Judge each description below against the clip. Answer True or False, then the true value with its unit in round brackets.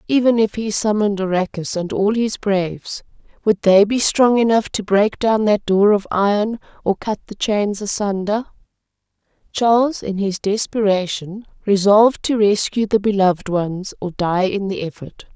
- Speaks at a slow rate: False (160 wpm)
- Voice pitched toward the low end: False (205 Hz)